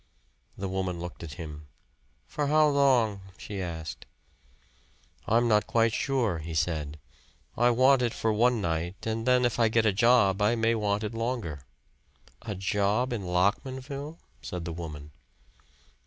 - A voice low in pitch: Yes, low, 105 Hz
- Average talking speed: Yes, average, 155 wpm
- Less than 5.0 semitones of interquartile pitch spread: No, wide, 5.5 semitones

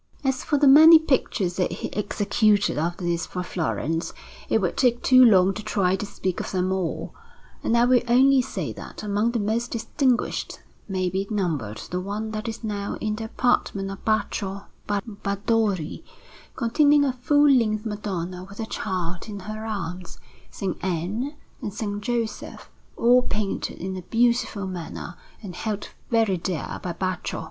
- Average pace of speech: Yes, average, 165 wpm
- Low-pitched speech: No, high, 210 Hz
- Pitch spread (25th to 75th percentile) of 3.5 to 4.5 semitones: Yes, average, 4.0 semitones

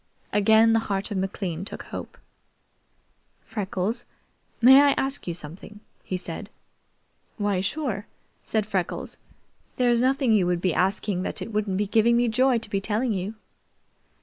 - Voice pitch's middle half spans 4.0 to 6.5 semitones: No, average, 3.6 semitones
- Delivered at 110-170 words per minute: Yes, average, 150 wpm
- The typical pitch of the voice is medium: No, high, 210 Hz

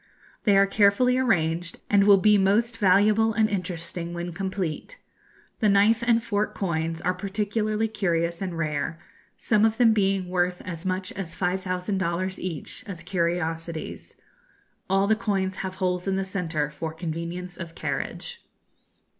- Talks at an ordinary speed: Yes, average, 150 wpm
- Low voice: No, high, 190 Hz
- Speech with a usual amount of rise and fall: Yes, average, 3.2 semitones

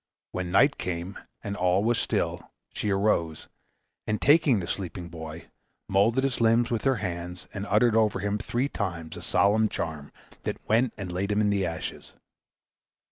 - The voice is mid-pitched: No, low, 100 Hz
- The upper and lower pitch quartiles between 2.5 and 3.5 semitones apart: No, average, 4.1 semitones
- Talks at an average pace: Yes, average, 170 wpm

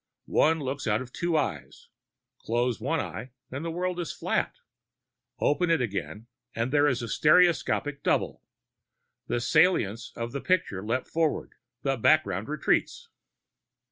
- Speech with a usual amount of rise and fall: No, wide, 5.7 semitones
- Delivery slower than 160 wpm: Yes, average, 140 wpm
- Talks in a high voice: No, medium, 140 Hz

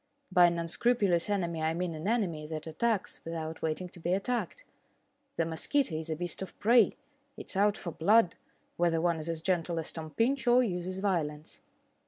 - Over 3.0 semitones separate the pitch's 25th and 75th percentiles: Yes, average, 3.9 semitones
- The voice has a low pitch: No, medium, 175 Hz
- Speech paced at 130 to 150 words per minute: No, average, 190 wpm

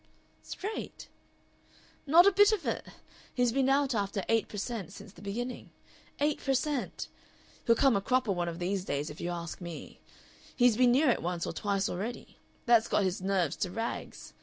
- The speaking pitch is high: Yes, high, 225 Hz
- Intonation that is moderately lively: No, wide, 5.7 semitones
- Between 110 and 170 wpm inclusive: No, average, 185 wpm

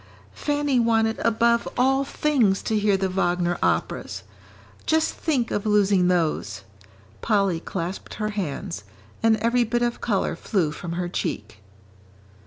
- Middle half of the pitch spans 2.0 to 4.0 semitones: No, average, 4.8 semitones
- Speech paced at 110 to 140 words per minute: Yes, slow, 135 wpm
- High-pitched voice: Yes, high, 210 Hz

